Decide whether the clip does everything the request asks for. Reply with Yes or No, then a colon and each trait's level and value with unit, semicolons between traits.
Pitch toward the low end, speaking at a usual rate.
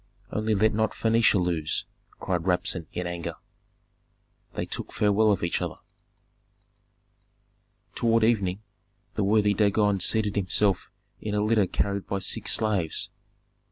No: low, 100 Hz; slow, 125 wpm